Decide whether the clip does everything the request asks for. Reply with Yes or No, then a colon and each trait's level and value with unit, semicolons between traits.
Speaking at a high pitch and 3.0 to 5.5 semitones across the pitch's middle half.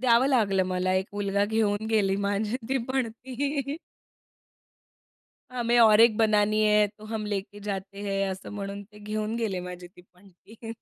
No: high, 210 Hz; narrow, 2.4 semitones